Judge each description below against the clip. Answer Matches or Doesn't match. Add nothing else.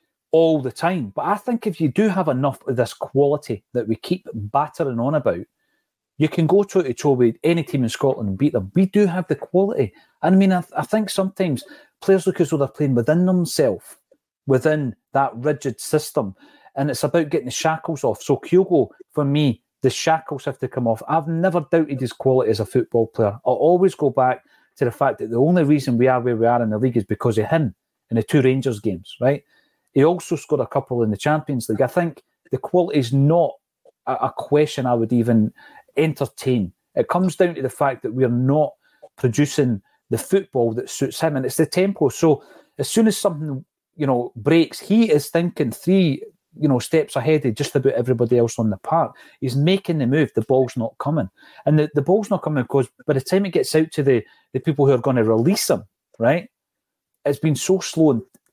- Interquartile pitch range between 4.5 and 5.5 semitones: Matches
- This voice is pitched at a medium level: Matches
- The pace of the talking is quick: Matches